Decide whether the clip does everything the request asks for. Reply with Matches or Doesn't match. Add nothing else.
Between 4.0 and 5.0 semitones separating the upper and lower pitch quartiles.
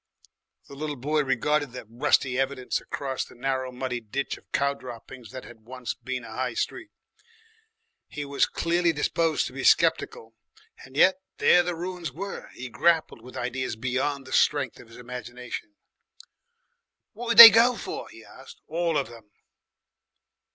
Matches